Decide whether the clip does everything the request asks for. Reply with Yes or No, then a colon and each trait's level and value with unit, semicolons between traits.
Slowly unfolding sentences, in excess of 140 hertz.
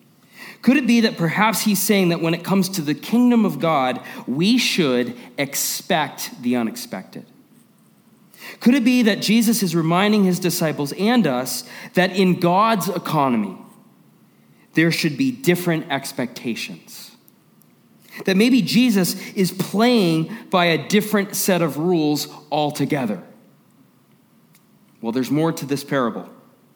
Yes: slow, 130 wpm; high, 190 Hz